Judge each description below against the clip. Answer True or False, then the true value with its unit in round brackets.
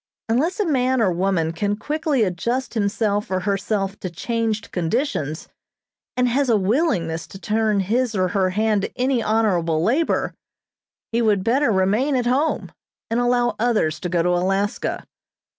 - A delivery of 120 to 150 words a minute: False (160 wpm)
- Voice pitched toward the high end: True (215 Hz)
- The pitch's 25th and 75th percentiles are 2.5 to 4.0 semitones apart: False (4.7 semitones)